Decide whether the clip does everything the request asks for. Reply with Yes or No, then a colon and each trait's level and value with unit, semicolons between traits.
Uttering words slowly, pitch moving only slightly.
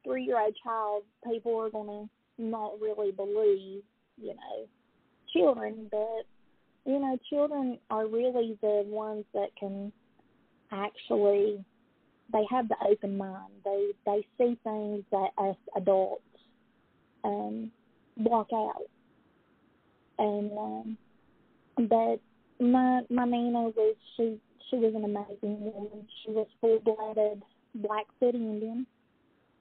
Yes: slow, 110 wpm; narrow, 2.2 semitones